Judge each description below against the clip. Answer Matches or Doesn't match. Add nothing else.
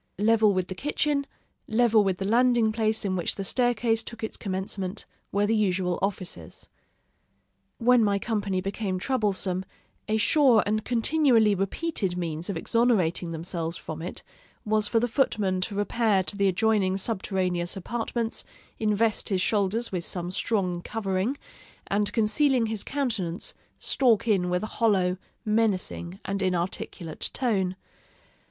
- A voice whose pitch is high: Matches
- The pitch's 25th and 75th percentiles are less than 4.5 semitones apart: Matches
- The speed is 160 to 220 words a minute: Doesn't match